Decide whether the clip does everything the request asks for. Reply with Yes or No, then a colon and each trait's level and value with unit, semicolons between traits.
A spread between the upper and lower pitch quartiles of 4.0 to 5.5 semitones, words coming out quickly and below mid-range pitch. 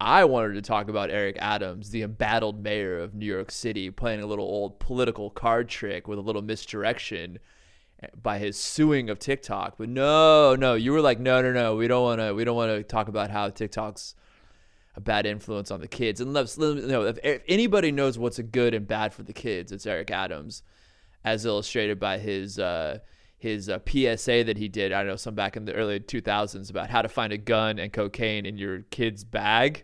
No: average, 2.7 semitones; fast, 215 wpm; low, 110 Hz